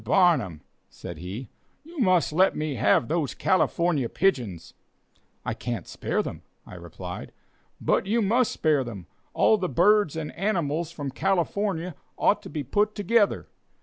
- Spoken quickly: No, average, 145 wpm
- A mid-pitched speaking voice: Yes, medium, 165 Hz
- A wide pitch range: Yes, wide, 7.4 semitones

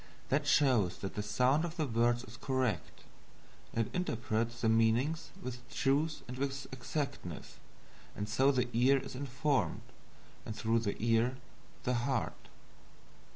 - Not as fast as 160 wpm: Yes, average, 140 wpm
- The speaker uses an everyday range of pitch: Yes, average, 3.3 semitones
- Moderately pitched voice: No, low, 125 Hz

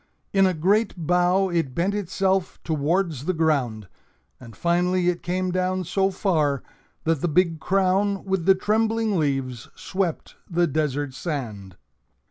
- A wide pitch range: No, average, 4.2 semitones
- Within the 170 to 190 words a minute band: No, average, 140 wpm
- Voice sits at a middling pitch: Yes, medium, 175 Hz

